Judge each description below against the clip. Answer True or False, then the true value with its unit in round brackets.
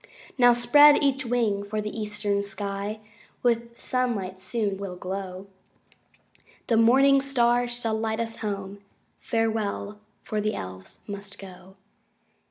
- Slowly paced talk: True (125 wpm)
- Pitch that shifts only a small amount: False (3.1 semitones)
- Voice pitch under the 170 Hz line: False (215 Hz)